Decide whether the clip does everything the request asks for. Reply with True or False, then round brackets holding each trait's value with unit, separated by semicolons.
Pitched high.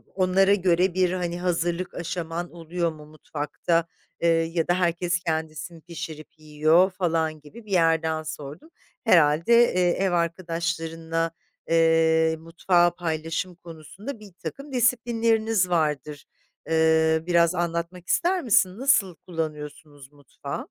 False (170 Hz)